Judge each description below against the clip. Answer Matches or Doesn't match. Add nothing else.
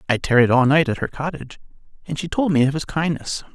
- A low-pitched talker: Doesn't match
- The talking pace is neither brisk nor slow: Doesn't match